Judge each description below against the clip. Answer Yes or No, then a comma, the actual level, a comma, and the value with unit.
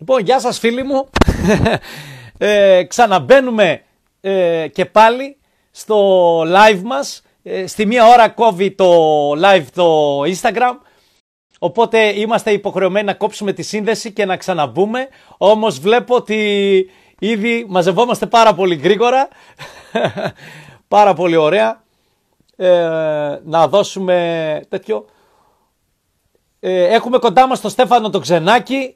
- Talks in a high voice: Yes, high, 205 Hz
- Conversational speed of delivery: No, slow, 100 wpm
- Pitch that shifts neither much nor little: Yes, average, 4.3 semitones